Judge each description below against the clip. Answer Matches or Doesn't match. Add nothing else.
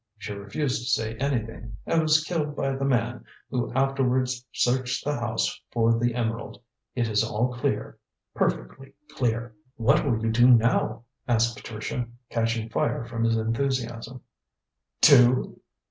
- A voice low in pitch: Matches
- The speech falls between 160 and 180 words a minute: Doesn't match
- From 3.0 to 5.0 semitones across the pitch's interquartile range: Doesn't match